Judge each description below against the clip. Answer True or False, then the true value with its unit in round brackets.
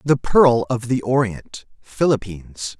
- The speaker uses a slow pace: True (105 wpm)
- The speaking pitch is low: True (120 Hz)